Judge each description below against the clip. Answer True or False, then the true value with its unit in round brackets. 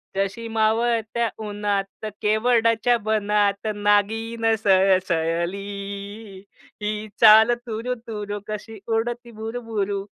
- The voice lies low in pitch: False (215 Hz)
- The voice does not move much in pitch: True (2.0 semitones)